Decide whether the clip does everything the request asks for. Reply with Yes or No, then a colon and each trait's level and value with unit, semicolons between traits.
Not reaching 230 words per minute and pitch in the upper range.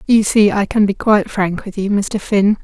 No: fast, 250 wpm; high, 205 Hz